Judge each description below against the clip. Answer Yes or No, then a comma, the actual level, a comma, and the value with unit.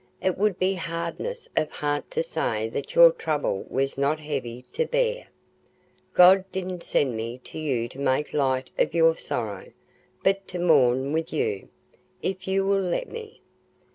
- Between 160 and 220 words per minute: Yes, average, 165 wpm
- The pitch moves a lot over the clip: Yes, wide, 5.9 semitones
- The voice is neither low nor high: Yes, medium, 165 Hz